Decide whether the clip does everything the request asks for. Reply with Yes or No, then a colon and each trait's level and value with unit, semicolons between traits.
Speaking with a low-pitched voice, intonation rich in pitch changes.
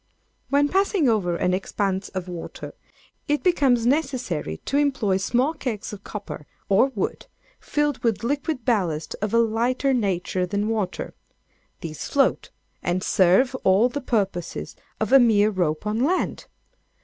No: high, 220 Hz; wide, 6.1 semitones